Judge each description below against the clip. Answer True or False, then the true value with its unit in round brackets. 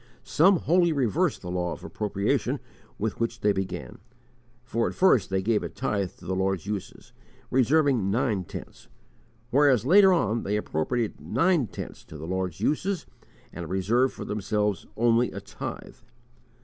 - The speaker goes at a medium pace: True (155 wpm)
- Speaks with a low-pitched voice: True (110 Hz)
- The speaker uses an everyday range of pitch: False (5.7 semitones)